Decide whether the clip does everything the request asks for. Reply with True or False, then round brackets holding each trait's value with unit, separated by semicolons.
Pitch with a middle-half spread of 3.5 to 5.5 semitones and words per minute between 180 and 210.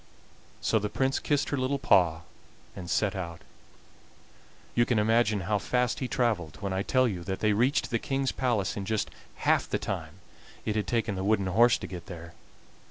True (4.5 semitones; 190 wpm)